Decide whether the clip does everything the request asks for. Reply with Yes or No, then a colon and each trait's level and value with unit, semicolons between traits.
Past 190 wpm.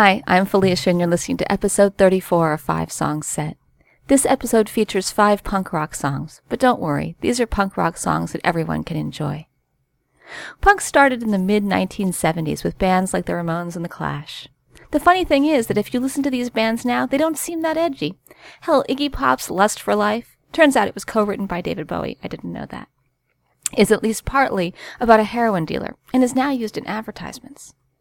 Yes: average, 200 wpm